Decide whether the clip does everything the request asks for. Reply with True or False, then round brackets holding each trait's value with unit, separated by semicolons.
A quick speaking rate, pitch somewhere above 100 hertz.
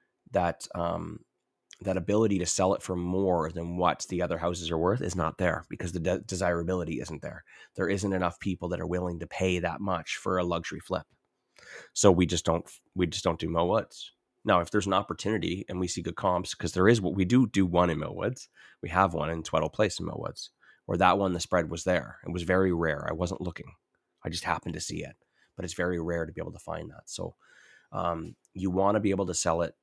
False (235 wpm; 90 Hz)